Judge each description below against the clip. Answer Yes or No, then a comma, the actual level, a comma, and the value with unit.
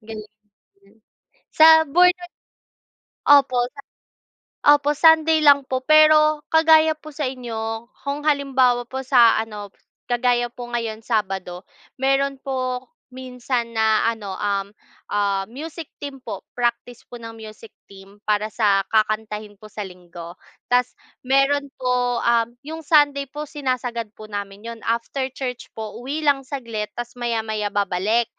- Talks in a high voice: Yes, high, 245 Hz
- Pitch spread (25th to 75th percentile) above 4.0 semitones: Yes, average, 4.5 semitones